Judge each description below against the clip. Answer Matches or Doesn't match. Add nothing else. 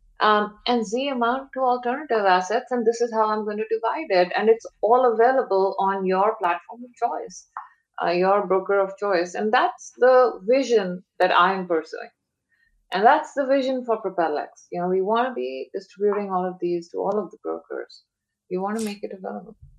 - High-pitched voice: Matches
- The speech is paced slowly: Doesn't match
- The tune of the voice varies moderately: Matches